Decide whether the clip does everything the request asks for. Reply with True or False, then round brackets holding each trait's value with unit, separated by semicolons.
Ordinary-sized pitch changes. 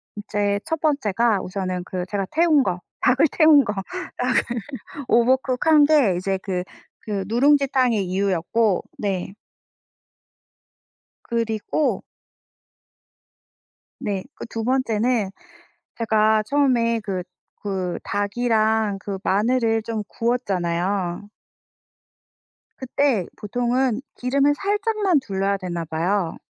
True (4.7 semitones)